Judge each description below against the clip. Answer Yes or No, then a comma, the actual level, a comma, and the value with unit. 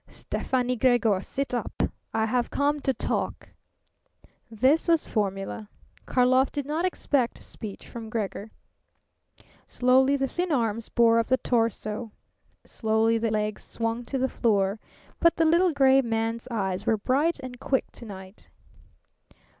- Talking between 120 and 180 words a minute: Yes, average, 140 wpm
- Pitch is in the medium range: No, high, 240 Hz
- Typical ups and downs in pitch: Yes, average, 3.4 semitones